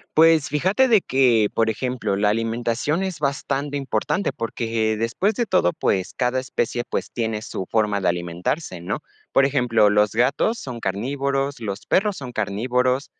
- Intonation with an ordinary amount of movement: Yes, average, 4.5 semitones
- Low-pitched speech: Yes, low, 125 Hz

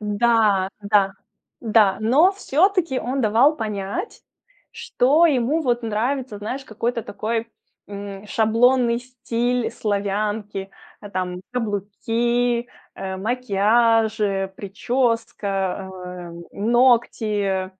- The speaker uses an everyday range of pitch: Yes, average, 3.4 semitones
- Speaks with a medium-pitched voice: No, high, 225 Hz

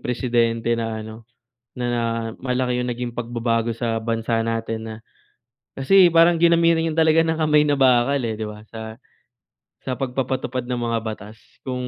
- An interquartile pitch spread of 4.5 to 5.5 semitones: No, average, 3.1 semitones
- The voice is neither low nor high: No, low, 120 Hz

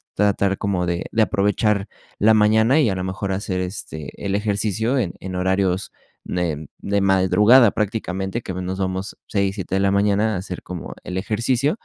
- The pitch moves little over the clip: Yes, narrow, 2.3 semitones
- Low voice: Yes, low, 100 Hz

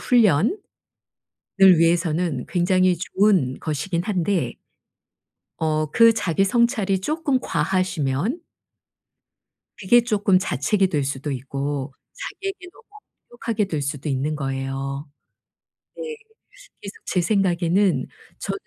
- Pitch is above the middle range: No, medium, 180 Hz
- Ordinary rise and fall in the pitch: No, wide, 6.0 semitones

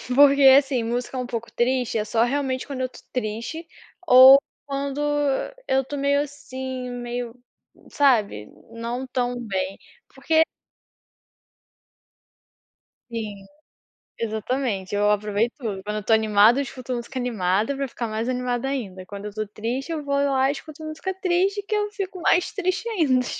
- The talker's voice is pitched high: Yes, very high, 250 Hz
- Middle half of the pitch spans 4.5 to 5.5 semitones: No, average, 4.1 semitones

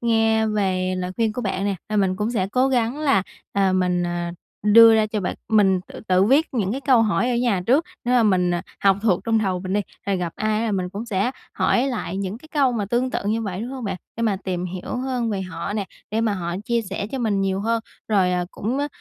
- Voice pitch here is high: Yes, high, 210 Hz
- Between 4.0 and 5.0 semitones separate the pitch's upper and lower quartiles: No, average, 3.6 semitones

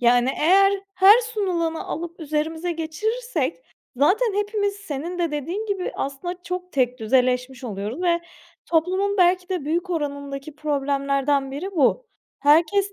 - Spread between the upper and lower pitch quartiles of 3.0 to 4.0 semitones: No, average, 5.2 semitones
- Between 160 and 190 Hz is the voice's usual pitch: No, very high, 330 Hz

